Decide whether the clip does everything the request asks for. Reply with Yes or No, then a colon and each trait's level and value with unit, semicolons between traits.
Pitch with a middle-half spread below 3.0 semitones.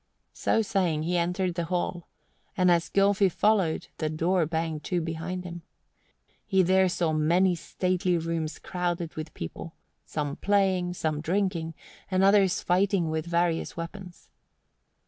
Yes: narrow, 2.4 semitones